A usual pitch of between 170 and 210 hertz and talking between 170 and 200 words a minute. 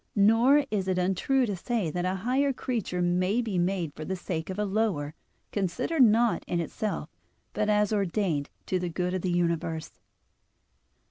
Yes: high, 190 Hz; average, 175 wpm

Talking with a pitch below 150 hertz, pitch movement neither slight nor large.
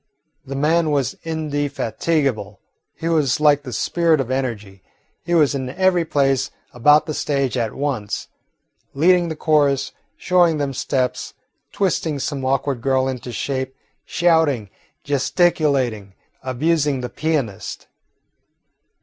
Yes: medium, 140 Hz; average, 3.4 semitones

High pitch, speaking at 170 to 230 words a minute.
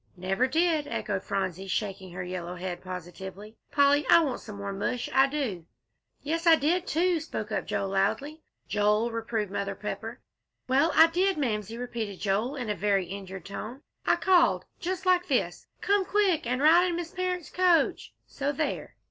Yes: high, 245 Hz; average, 175 wpm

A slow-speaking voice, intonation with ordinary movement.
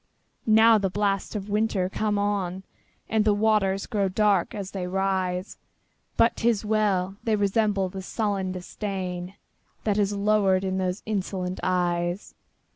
No: slow, 130 wpm; narrow, 2.2 semitones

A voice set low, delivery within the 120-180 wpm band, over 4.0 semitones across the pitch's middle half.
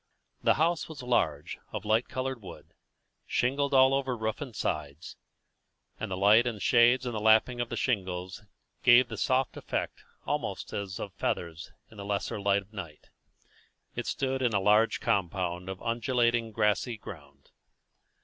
Yes: low, 110 Hz; average, 160 wpm; average, 4.5 semitones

